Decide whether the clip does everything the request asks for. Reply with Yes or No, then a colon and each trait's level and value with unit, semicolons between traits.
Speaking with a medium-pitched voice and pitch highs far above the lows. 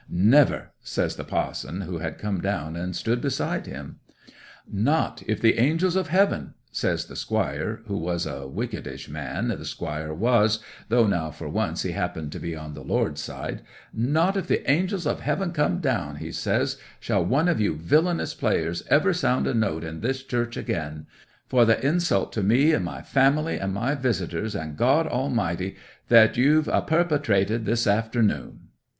No: low, 115 Hz; wide, 8.6 semitones